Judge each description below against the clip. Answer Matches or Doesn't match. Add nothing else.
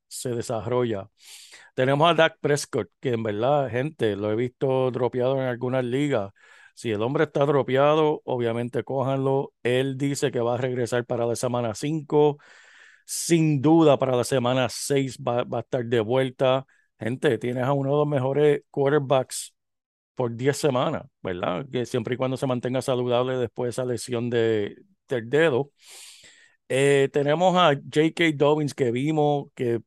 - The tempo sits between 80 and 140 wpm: Doesn't match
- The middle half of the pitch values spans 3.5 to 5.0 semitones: Doesn't match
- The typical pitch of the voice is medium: Doesn't match